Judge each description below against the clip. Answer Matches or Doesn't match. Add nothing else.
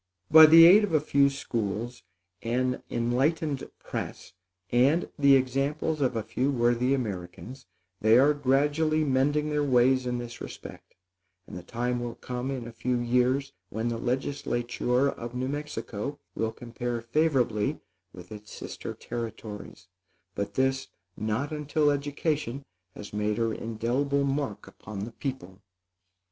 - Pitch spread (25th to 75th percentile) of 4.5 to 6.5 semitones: Doesn't match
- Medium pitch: Doesn't match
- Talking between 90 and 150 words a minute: Matches